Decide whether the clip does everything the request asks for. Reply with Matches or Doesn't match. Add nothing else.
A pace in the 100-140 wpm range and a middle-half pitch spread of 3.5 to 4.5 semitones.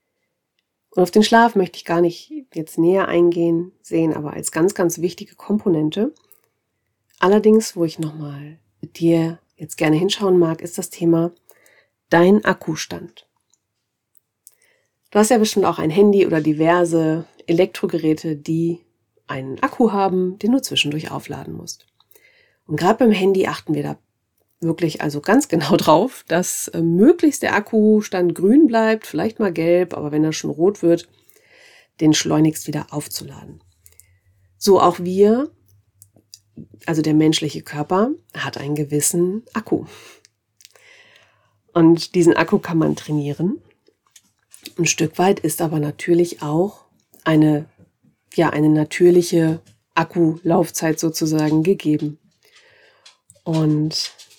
Matches